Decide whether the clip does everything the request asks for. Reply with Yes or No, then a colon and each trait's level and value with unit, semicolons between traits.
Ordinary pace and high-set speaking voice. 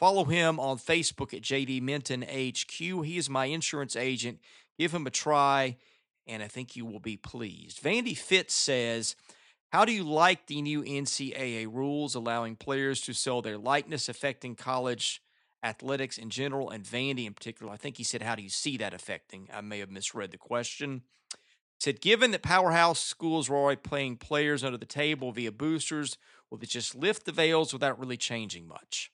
No: average, 185 wpm; low, 135 Hz